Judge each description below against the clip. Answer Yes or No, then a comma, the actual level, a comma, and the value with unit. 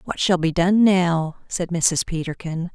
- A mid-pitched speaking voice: Yes, medium, 175 Hz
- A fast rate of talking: No, average, 175 wpm